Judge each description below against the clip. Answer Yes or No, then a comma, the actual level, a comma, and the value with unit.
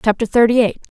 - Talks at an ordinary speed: Yes, average, 180 wpm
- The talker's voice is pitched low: No, high, 225 Hz